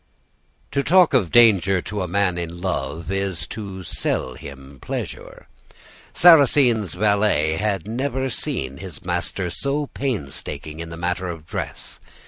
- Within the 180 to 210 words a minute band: No, slow, 135 wpm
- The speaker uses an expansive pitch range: Yes, wide, 5.9 semitones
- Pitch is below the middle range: Yes, very low, 95 Hz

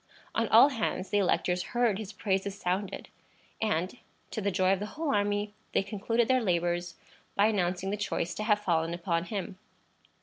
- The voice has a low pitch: No, high, 200 Hz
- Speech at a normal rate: Yes, average, 175 wpm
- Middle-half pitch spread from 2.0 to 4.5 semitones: Yes, average, 2.9 semitones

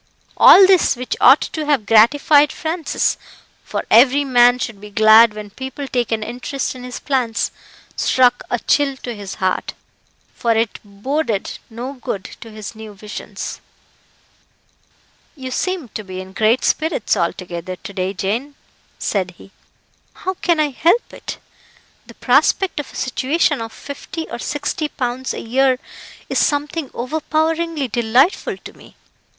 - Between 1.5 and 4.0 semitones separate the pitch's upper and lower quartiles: No, average, 5.1 semitones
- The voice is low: No, very high, 250 Hz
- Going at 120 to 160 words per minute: Yes, average, 150 wpm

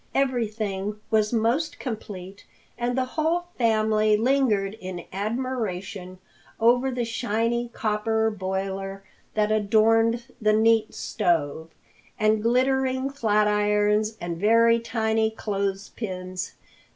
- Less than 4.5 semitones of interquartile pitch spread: Yes, average, 2.7 semitones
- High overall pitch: Yes, high, 215 Hz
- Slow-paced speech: Yes, slow, 105 wpm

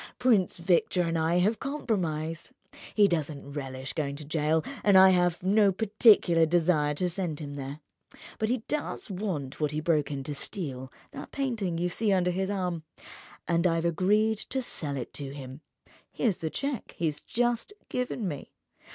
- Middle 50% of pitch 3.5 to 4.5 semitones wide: No, average, 5.1 semitones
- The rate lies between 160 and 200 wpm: Yes, average, 165 wpm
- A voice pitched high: No, medium, 170 Hz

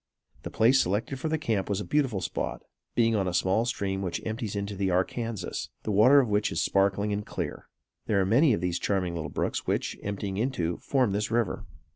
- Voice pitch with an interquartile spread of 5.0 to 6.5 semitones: No, average, 3.4 semitones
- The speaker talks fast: Yes, fast, 210 wpm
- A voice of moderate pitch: No, low, 105 Hz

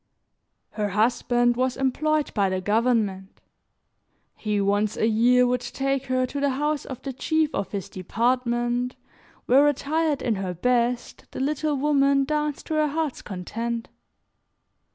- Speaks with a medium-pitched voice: No, very high, 250 Hz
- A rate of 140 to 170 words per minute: Yes, average, 145 wpm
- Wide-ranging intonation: No, average, 4.2 semitones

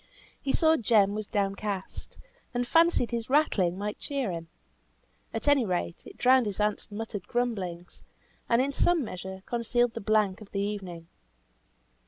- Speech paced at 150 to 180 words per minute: Yes, average, 155 wpm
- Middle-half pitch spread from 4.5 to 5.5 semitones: No, average, 3.9 semitones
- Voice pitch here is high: Yes, high, 215 Hz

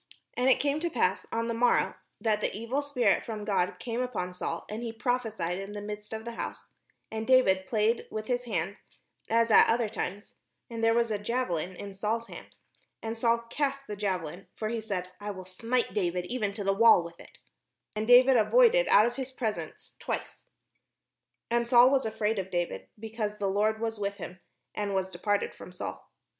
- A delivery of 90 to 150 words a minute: No, average, 200 wpm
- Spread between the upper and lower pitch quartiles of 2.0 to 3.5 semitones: Yes, average, 3.1 semitones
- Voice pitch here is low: No, high, 220 Hz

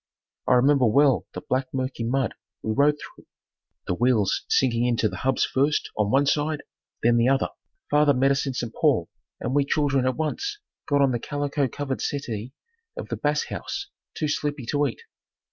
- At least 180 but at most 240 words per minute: Yes, average, 190 wpm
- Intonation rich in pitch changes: No, average, 2.8 semitones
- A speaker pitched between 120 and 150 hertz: Yes, low, 135 Hz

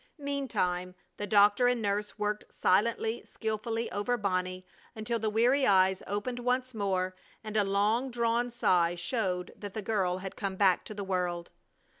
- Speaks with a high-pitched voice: Yes, high, 210 Hz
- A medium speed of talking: Yes, average, 160 wpm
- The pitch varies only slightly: No, average, 3.8 semitones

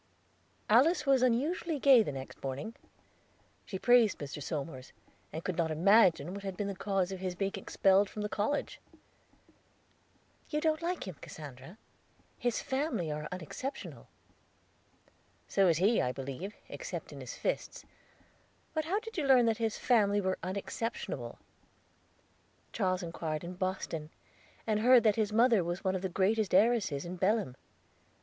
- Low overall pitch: No, high, 200 Hz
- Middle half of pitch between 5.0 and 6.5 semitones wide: Yes, wide, 5.5 semitones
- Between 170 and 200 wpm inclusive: No, average, 155 wpm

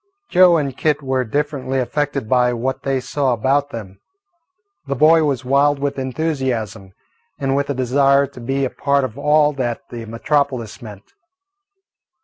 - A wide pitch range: No, narrow, 2.5 semitones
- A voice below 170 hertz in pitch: Yes, low, 135 Hz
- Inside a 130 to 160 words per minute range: Yes, average, 155 wpm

